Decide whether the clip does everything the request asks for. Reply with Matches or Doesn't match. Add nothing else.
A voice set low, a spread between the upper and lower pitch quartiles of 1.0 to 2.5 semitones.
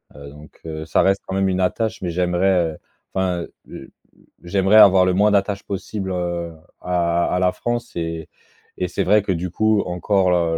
Matches